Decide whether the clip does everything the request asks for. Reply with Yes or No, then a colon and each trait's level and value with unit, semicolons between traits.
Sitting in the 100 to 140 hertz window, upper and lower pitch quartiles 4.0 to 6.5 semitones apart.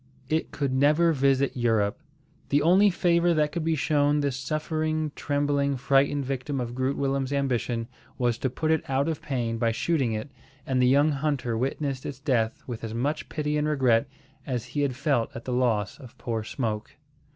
No: low, 135 Hz; average, 3.4 semitones